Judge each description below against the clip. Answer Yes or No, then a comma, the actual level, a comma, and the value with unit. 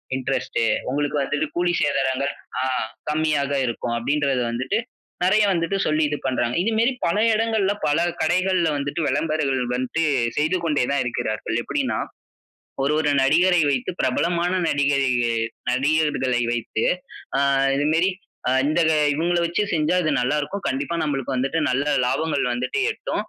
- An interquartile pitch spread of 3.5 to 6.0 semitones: Yes, average, 4.1 semitones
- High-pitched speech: No, medium, 145 Hz